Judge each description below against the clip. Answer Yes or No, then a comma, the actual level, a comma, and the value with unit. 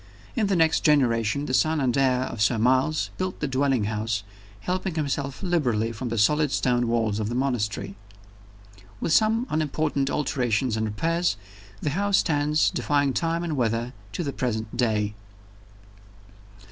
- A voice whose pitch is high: No, low, 135 Hz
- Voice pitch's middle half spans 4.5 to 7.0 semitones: Yes, average, 5.2 semitones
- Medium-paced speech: Yes, average, 155 wpm